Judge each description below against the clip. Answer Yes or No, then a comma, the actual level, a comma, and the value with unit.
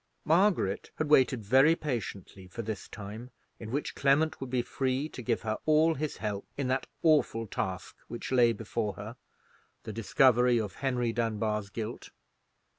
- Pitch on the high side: No, low, 120 Hz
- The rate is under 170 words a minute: Yes, average, 155 wpm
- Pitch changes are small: No, average, 4.0 semitones